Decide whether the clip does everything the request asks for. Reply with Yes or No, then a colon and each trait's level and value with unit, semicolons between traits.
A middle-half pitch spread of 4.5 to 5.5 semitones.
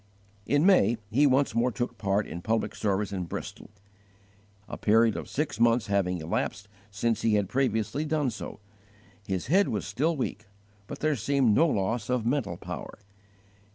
Yes: average, 5.1 semitones